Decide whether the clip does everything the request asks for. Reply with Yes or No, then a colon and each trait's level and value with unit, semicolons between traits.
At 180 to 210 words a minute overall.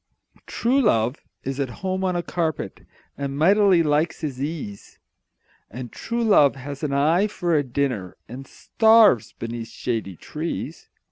No: average, 145 wpm